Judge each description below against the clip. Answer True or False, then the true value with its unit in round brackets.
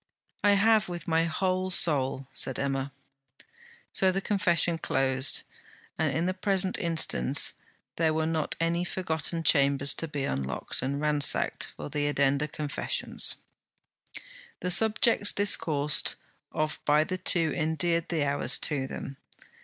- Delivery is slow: True (130 wpm)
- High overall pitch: False (160 Hz)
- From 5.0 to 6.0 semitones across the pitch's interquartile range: False (4.1 semitones)